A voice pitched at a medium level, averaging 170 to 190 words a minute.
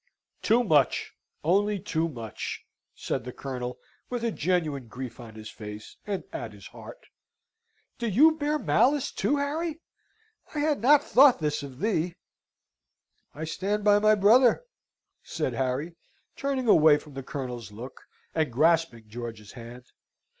No: medium, 160 Hz; average, 145 wpm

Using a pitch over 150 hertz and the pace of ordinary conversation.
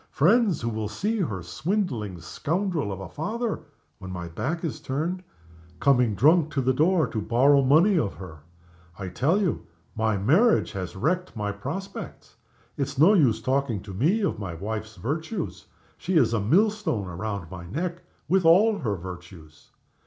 No: low, 135 Hz; average, 165 wpm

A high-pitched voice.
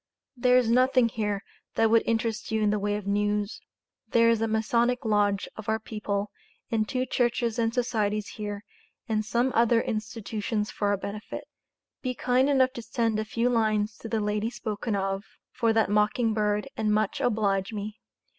Yes: high, 220 Hz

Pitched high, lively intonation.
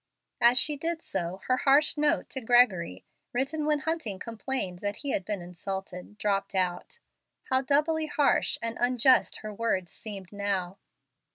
Yes: high, 230 Hz; wide, 6.5 semitones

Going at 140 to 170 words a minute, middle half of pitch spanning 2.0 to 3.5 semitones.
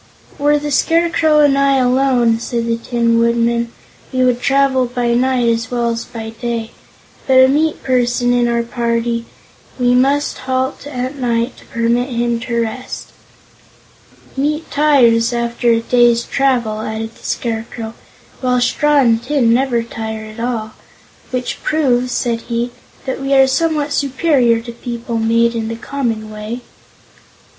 Yes: average, 155 wpm; narrow, 2.4 semitones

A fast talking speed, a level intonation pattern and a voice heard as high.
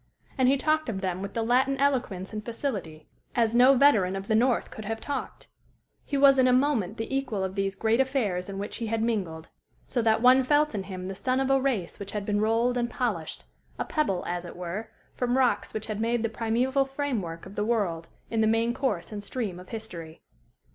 No: fast, 225 wpm; average, 4.7 semitones; high, 225 Hz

